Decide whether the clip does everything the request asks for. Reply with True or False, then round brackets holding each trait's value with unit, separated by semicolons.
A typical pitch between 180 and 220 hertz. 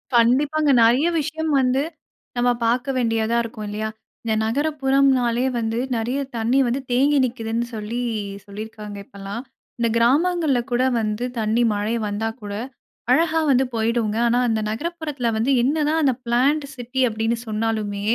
False (235 Hz)